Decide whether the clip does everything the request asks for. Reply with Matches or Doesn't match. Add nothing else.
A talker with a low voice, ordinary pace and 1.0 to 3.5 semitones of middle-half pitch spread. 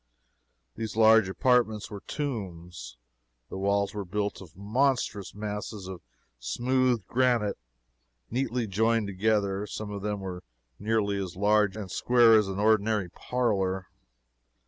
Doesn't match